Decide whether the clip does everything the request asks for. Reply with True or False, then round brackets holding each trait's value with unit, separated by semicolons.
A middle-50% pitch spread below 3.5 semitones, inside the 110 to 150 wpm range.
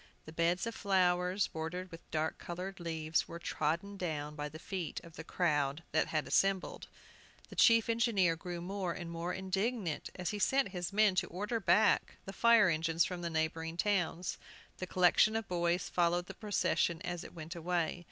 False (2.9 semitones; 180 wpm)